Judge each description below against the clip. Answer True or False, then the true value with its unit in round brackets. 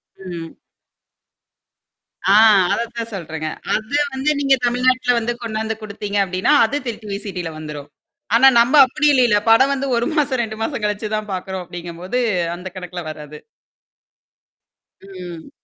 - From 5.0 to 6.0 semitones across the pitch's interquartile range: True (5.4 semitones)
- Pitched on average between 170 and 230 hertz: True (215 Hz)